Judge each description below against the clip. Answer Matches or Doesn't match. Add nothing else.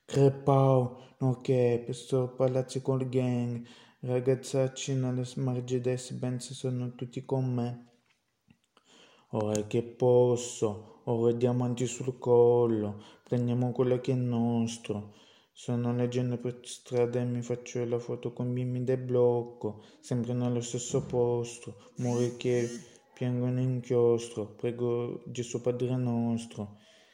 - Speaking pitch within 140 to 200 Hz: Doesn't match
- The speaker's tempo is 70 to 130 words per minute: Matches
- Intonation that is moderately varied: Doesn't match